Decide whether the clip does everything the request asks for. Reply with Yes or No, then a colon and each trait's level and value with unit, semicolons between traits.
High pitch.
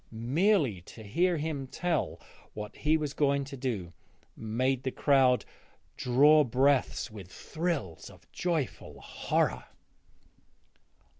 No: low, 135 Hz